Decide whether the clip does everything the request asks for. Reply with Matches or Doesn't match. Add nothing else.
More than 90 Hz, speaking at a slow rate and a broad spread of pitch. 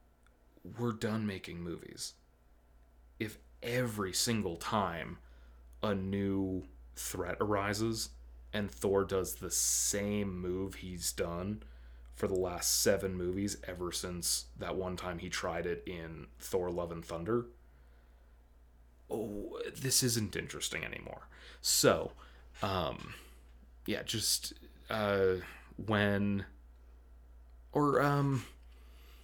Doesn't match